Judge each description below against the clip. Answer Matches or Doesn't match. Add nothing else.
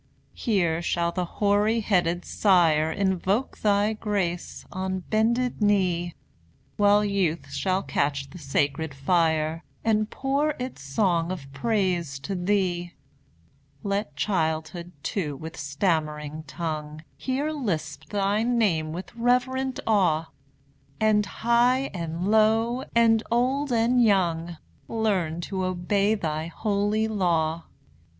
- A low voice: Doesn't match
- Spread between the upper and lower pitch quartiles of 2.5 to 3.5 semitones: Doesn't match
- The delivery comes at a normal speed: Doesn't match